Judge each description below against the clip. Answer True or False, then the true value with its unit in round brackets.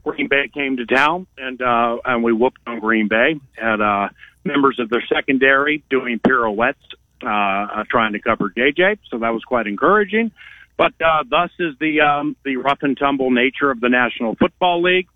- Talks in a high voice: False (130 Hz)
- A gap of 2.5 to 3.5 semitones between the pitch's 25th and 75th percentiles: False (4.2 semitones)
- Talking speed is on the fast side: False (185 wpm)